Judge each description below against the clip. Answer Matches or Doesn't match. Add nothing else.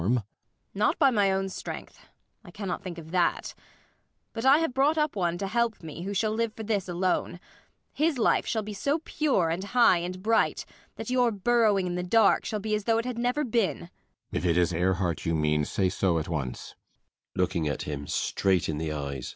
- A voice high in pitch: Matches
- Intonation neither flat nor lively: Matches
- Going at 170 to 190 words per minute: Doesn't match